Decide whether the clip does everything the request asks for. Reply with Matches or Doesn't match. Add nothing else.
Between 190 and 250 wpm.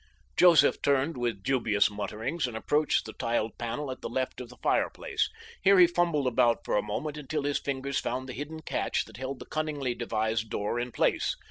Matches